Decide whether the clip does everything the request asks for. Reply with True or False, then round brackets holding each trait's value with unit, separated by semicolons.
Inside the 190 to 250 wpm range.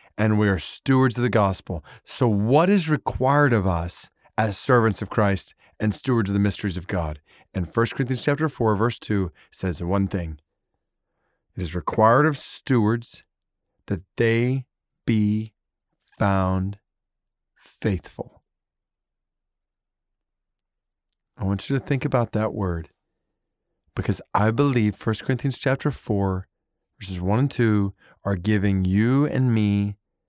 False (135 wpm)